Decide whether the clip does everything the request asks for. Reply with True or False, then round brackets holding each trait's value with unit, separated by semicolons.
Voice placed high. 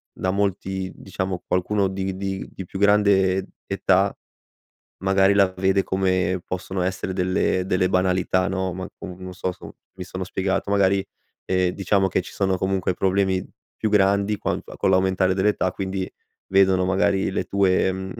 False (95 Hz)